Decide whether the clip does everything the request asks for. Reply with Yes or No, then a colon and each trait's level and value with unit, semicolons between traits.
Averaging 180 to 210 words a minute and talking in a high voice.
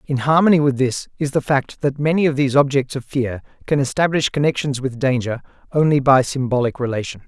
No: average, 190 wpm; low, 135 Hz